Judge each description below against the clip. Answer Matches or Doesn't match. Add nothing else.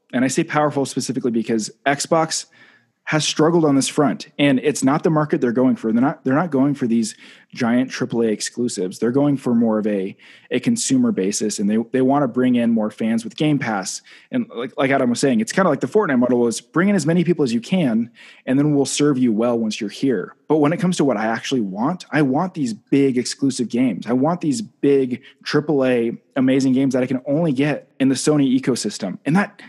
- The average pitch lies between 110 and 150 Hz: Matches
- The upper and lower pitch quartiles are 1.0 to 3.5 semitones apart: Doesn't match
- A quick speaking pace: Matches